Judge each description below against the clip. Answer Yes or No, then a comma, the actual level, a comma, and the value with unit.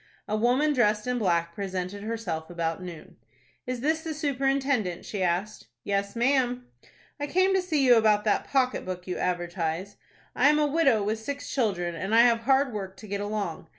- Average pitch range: No, wide, 6.3 semitones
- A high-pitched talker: Yes, high, 215 Hz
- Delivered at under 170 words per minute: No, average, 185 wpm